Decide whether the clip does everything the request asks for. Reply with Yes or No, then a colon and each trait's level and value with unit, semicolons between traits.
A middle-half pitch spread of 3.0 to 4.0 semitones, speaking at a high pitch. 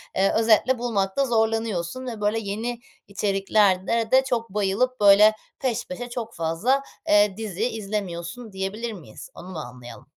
Yes: average, 3.4 semitones; high, 215 Hz